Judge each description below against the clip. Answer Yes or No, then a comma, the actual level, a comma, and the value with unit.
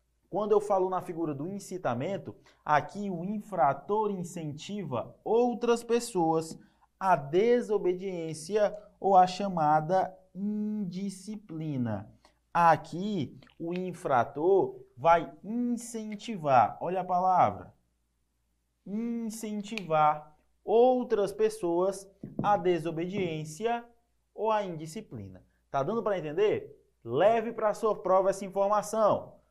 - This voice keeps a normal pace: No, slow, 95 wpm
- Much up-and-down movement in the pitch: No, average, 4.6 semitones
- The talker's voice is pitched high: Yes, high, 195 Hz